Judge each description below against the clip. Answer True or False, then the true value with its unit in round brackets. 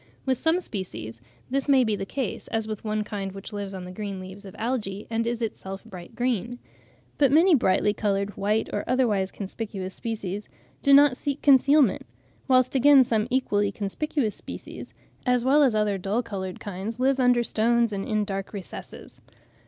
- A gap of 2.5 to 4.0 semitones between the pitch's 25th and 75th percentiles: False (4.4 semitones)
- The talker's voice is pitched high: True (215 Hz)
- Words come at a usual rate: True (175 wpm)